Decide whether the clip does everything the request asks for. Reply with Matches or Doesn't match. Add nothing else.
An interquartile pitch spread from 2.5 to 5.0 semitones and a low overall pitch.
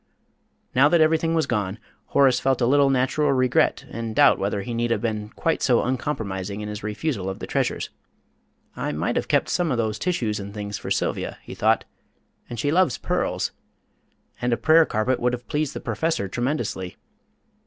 Doesn't match